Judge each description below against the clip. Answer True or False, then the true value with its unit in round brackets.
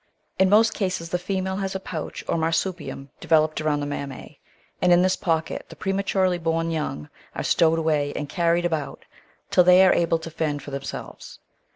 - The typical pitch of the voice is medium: True (165 Hz)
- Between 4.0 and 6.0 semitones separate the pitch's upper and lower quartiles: False (3.2 semitones)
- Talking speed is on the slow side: False (185 wpm)